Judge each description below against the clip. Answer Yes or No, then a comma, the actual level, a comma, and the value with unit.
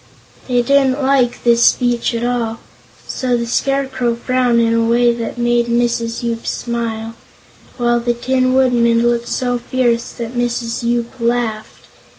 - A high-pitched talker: Yes, high, 240 Hz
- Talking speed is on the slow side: No, average, 150 wpm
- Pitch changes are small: Yes, narrow, 1.0 semitones